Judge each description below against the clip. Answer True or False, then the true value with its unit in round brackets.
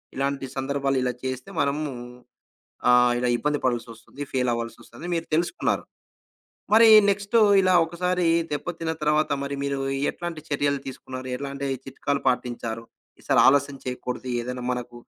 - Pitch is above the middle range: False (140 Hz)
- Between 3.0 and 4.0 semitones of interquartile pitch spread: True (3.5 semitones)